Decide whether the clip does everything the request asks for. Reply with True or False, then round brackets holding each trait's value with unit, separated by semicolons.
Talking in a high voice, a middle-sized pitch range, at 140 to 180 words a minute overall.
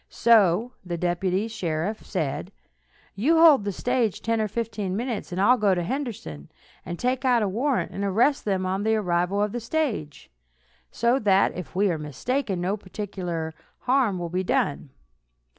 True (200 Hz; 4.7 semitones; 170 wpm)